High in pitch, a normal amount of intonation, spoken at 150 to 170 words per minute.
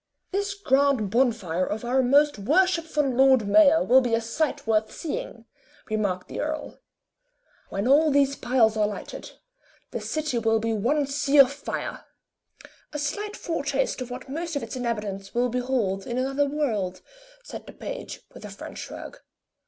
Yes: very high, 260 Hz; average, 4.9 semitones; average, 160 wpm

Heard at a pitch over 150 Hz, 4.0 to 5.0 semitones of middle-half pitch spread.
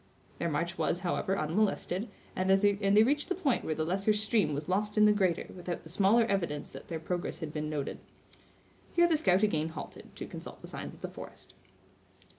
Yes: high, 190 Hz; average, 4.4 semitones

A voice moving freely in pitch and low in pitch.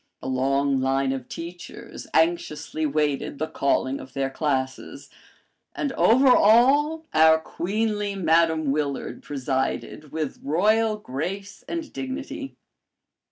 No: wide, 7.4 semitones; medium, 160 Hz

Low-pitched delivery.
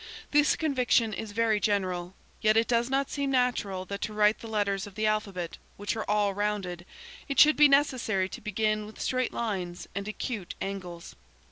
No: high, 215 Hz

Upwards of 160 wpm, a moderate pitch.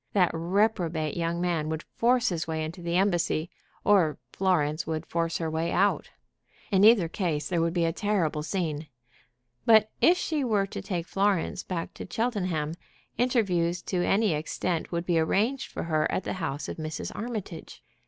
Yes: average, 175 wpm; medium, 175 Hz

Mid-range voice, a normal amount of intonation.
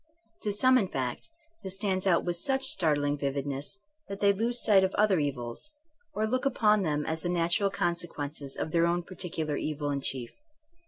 No: medium, 175 Hz; wide, 5.7 semitones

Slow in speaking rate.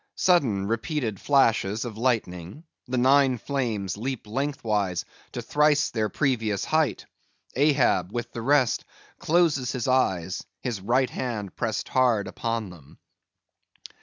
Yes: slow, 125 wpm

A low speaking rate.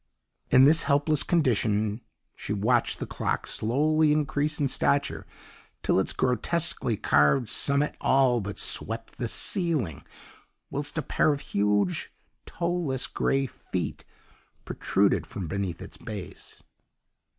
Yes: slow, 120 wpm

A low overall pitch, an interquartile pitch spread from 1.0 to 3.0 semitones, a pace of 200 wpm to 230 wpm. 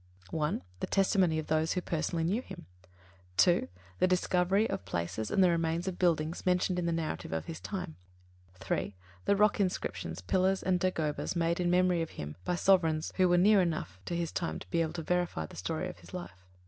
No: medium, 170 Hz; average, 2.7 semitones; fast, 205 wpm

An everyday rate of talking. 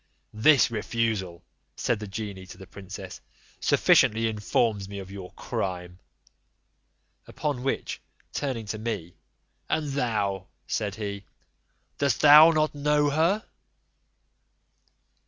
No: slow, 110 wpm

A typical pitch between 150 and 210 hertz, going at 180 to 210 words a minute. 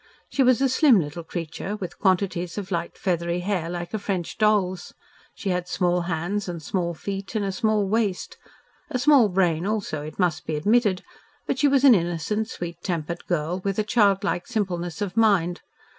Yes: medium, 185 Hz; average, 185 wpm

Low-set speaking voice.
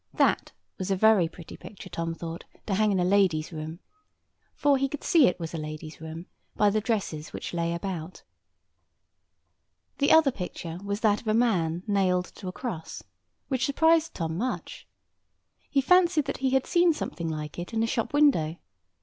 No: high, 195 Hz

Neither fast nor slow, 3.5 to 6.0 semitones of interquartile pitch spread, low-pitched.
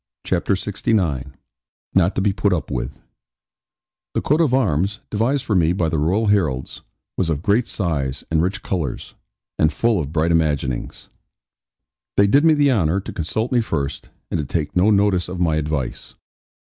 Yes: average, 175 wpm; average, 5.0 semitones; very low, 90 Hz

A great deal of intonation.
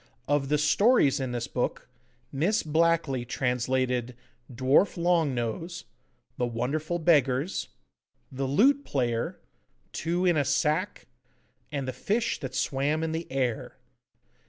No: average, 4.5 semitones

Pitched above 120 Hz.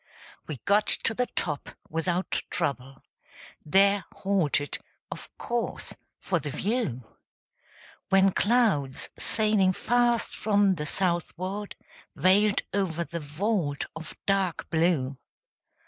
Yes: medium, 185 Hz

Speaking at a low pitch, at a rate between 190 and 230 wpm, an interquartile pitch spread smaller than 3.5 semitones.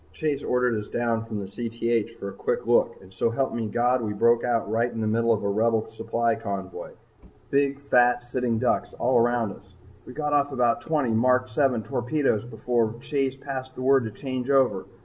Yes: low, 120 Hz; average, 200 wpm; narrow, 2.5 semitones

